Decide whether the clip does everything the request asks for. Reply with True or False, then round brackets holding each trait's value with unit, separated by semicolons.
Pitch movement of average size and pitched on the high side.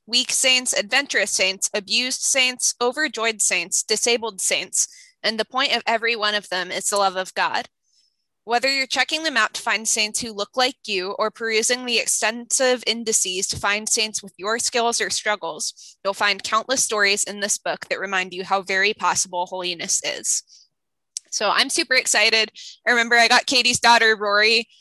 True (3.4 semitones; 220 Hz)